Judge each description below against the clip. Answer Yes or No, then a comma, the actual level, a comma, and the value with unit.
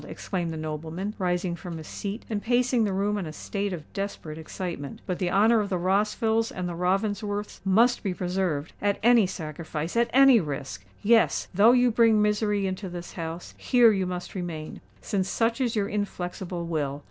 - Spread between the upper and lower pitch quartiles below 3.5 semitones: No, average, 3.8 semitones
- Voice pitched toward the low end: No, high, 190 Hz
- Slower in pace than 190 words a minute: Yes, average, 170 wpm